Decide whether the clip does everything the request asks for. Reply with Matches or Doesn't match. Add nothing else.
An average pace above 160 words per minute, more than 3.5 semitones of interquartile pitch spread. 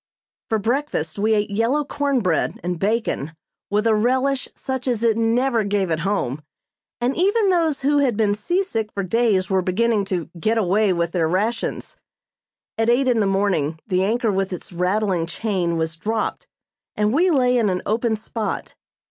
Matches